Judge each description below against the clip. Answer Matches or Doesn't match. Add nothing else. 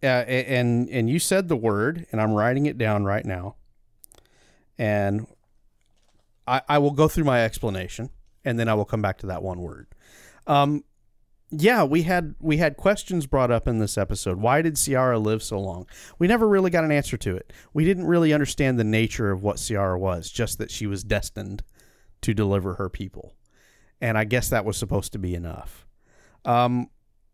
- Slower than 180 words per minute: Doesn't match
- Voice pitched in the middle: Doesn't match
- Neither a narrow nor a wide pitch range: Doesn't match